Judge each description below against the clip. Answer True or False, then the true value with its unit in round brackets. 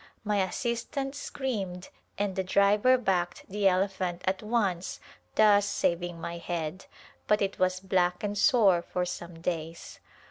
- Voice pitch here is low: False (190 Hz)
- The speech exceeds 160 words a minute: False (140 wpm)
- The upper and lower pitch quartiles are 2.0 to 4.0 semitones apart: True (2.8 semitones)